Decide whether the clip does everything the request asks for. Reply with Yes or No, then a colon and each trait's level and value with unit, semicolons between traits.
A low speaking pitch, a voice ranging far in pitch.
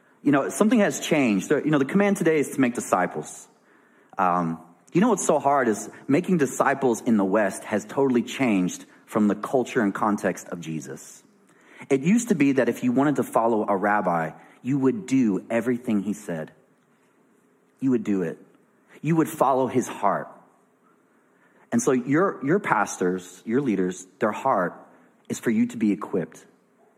Yes: low, 125 Hz; wide, 7.6 semitones